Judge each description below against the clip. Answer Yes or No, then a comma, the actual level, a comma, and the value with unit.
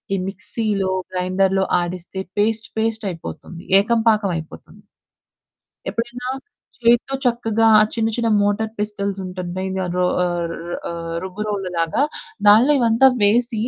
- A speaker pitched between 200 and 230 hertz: Yes, high, 205 Hz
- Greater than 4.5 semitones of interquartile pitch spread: No, average, 3.3 semitones